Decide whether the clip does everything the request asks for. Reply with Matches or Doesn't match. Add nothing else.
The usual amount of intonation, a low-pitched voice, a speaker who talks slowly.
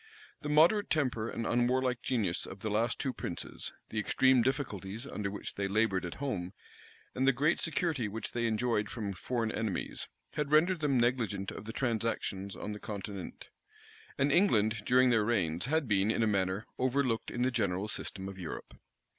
Doesn't match